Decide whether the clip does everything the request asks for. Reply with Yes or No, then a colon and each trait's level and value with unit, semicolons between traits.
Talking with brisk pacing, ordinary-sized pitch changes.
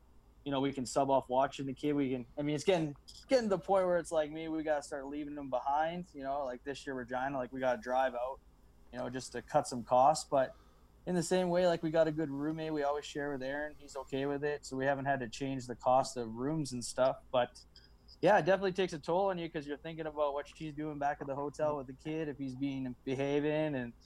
Yes: fast, 270 wpm; average, 3.0 semitones